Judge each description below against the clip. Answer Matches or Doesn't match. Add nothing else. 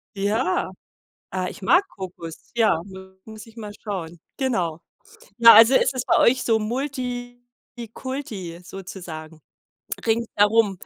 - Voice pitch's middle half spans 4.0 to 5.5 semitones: Matches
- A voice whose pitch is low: Doesn't match